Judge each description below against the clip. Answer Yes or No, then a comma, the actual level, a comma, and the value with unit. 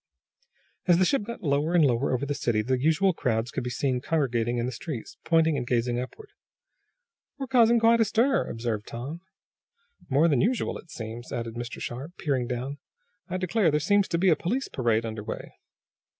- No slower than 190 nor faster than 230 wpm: Yes, average, 195 wpm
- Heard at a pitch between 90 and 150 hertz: Yes, medium, 140 Hz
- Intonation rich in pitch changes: Yes, wide, 6.9 semitones